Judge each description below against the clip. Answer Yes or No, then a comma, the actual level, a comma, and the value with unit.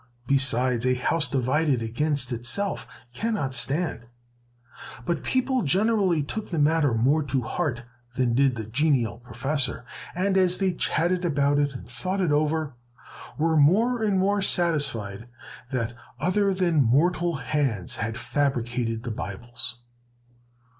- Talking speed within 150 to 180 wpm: No, slow, 135 wpm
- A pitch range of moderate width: No, wide, 6.3 semitones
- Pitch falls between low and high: Yes, medium, 145 Hz